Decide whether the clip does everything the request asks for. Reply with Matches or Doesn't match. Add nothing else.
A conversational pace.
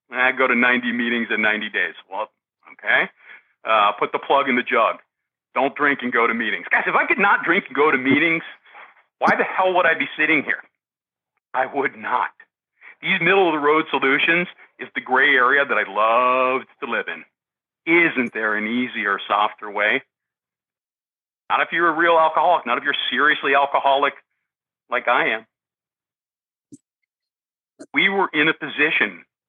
Matches